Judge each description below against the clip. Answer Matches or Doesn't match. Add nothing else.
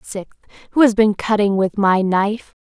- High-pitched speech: Matches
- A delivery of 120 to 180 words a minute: Doesn't match